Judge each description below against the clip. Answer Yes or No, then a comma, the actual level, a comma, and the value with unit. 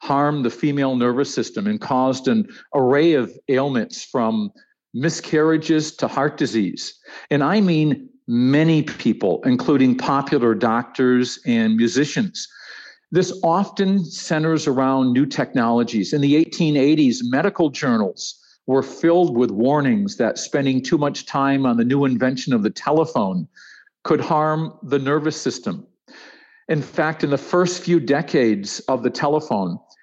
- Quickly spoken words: No, slow, 135 wpm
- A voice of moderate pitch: Yes, medium, 155 Hz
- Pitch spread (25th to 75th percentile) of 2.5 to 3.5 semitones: No, average, 5.1 semitones